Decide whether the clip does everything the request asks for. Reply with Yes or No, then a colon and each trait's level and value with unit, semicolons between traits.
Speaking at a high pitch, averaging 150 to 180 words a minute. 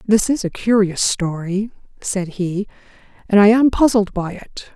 Yes: high, 200 Hz; average, 165 wpm